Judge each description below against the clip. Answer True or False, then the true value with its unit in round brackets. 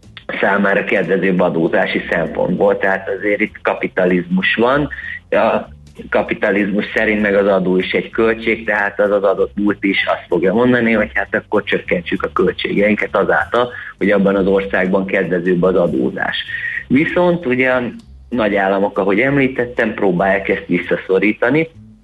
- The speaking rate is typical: True (140 wpm)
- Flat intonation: False (3.2 semitones)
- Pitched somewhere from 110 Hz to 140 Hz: False (100 Hz)